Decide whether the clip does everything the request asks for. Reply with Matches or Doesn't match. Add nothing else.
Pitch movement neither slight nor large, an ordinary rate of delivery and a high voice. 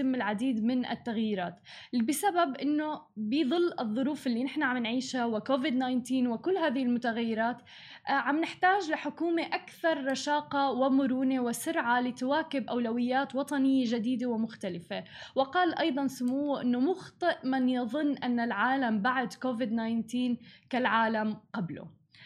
Matches